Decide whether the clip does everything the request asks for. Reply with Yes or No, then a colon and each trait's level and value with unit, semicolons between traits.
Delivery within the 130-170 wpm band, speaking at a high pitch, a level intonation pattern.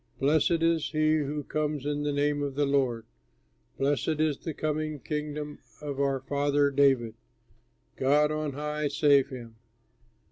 No: average, 145 wpm; medium, 145 Hz; narrow, 1.5 semitones